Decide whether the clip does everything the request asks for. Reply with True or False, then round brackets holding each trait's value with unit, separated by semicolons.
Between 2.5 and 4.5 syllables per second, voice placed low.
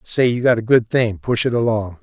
False (5.2 syllables/s; 115 Hz)